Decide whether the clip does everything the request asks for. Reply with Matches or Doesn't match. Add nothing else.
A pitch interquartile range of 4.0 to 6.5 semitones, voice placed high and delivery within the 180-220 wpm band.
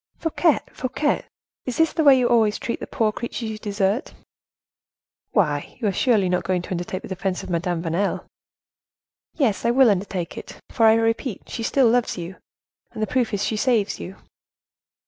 Matches